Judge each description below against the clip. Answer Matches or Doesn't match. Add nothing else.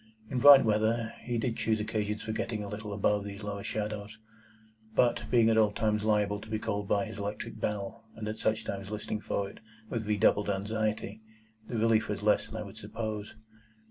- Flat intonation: Matches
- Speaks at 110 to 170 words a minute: Doesn't match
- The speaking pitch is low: Matches